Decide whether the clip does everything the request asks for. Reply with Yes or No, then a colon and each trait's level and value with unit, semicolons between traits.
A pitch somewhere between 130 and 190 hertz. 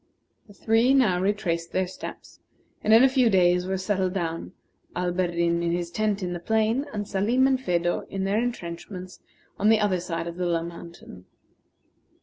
Yes: medium, 185 Hz